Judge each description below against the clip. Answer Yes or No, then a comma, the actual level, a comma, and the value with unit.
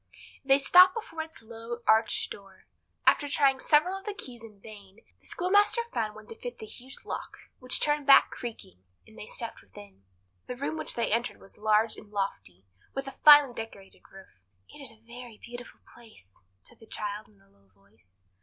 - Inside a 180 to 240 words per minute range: Yes, average, 190 wpm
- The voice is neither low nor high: No, high, 225 Hz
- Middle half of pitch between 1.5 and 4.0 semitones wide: No, wide, 5.4 semitones